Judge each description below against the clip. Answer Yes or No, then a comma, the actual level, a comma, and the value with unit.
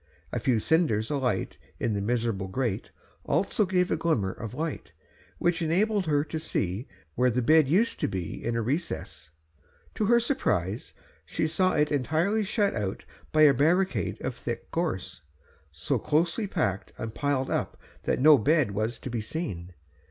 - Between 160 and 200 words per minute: Yes, average, 165 wpm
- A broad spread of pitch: Yes, wide, 7.2 semitones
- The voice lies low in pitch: No, medium, 145 Hz